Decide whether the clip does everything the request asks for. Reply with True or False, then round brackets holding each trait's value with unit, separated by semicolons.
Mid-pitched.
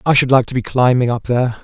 False (125 Hz)